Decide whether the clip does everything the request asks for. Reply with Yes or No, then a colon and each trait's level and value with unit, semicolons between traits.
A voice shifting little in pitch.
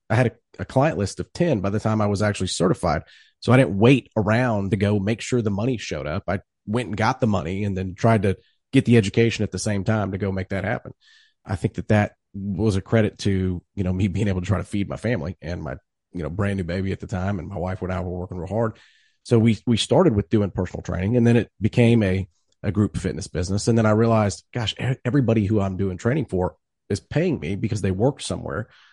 No: average, 3.3 semitones